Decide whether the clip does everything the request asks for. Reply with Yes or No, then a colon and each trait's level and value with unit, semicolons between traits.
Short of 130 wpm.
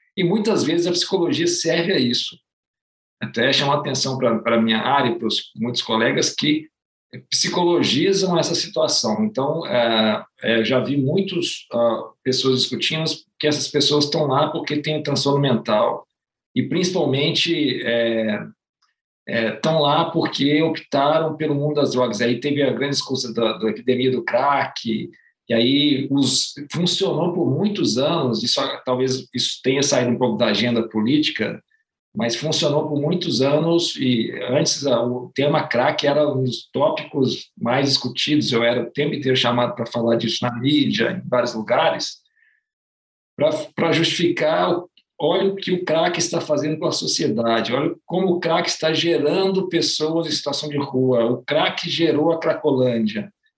No: average, 155 wpm